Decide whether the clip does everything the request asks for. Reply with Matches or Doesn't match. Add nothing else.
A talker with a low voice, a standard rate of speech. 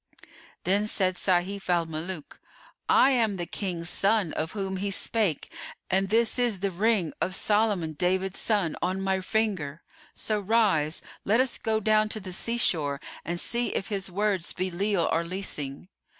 Doesn't match